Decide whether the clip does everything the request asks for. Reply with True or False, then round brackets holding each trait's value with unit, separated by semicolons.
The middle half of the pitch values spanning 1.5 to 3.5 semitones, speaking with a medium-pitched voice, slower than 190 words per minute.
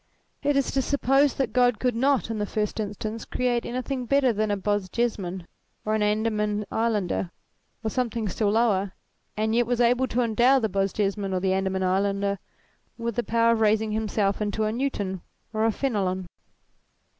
False (3.1 semitones; 220 Hz; 175 wpm)